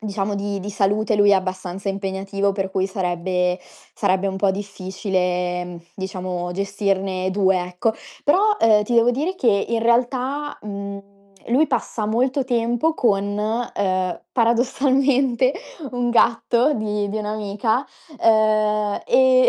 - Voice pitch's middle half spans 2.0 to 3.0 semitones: No, average, 3.7 semitones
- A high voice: Yes, high, 205 Hz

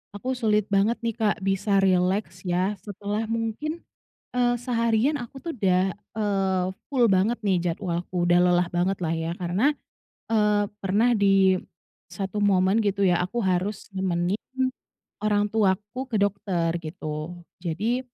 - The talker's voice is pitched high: Yes, high, 200 Hz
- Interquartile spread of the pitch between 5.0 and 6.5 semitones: No, average, 3.3 semitones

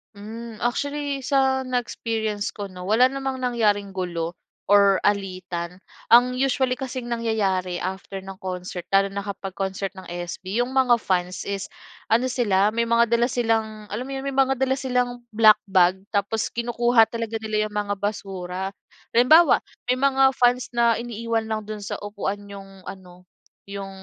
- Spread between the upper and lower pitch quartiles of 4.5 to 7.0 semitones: No, average, 4.0 semitones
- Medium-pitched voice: No, high, 215 Hz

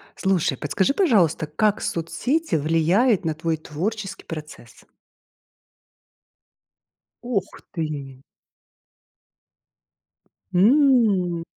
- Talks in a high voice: No, medium, 175 Hz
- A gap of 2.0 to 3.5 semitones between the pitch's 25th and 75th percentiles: No, wide, 5.6 semitones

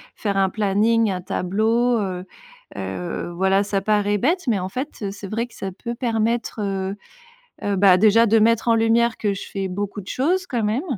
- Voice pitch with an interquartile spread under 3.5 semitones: Yes, average, 2.9 semitones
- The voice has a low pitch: No, high, 210 Hz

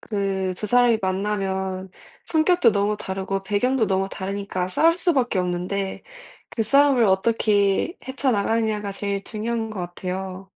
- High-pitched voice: Yes, high, 200 Hz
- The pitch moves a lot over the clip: No, average, 3.2 semitones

